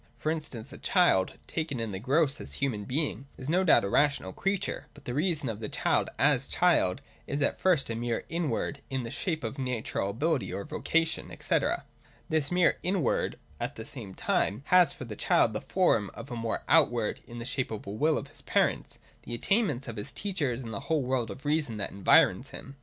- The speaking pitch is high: No, low, 135 Hz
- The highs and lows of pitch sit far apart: Yes, wide, 5.7 semitones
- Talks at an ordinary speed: No, fast, 215 wpm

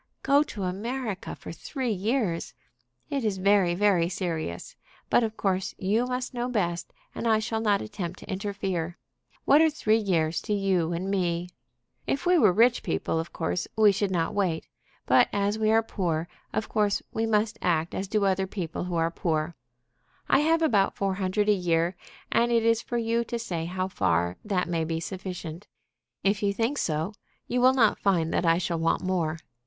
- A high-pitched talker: Yes, high, 195 Hz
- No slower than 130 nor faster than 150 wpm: No, average, 190 wpm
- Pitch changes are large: No, average, 4.3 semitones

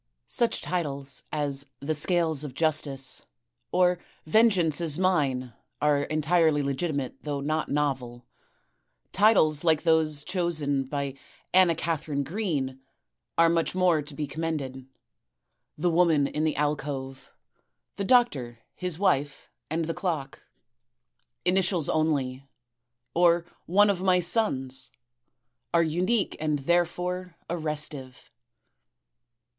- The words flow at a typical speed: No, slow, 110 wpm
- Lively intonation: No, average, 3.8 semitones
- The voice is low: No, medium, 155 Hz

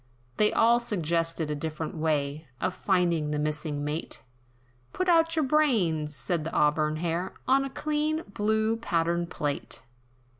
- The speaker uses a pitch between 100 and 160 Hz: No, medium, 170 Hz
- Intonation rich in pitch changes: Yes, wide, 6.8 semitones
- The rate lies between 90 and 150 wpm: Yes, average, 145 wpm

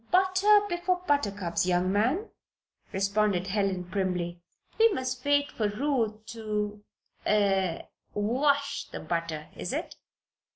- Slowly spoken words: Yes, slow, 115 wpm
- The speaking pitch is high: Yes, high, 210 Hz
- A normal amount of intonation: No, wide, 7.1 semitones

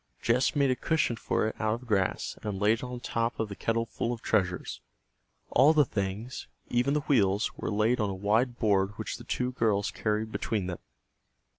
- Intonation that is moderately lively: Yes, average, 3.3 semitones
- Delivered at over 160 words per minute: Yes, average, 200 wpm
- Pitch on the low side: Yes, low, 110 Hz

